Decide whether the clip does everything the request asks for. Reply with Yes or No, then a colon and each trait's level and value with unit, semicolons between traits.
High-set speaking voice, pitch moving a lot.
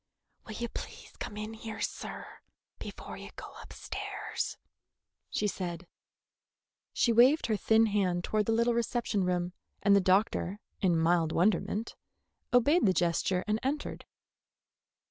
No: high, 210 Hz; average, 4.0 semitones